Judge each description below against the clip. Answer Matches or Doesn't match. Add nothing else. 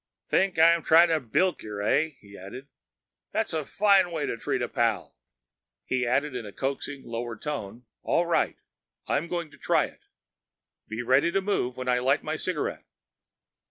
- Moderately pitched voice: Matches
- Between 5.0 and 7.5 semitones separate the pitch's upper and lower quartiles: Matches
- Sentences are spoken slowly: Doesn't match